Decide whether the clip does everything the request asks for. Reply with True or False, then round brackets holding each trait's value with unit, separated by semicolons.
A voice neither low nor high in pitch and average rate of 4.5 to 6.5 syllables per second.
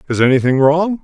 True (150 Hz; 6.0 syllables/s)